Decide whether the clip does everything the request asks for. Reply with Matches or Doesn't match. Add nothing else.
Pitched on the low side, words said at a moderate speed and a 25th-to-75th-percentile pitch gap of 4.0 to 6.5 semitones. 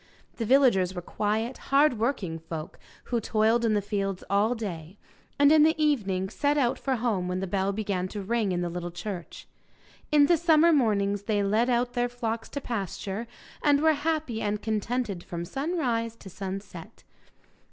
Doesn't match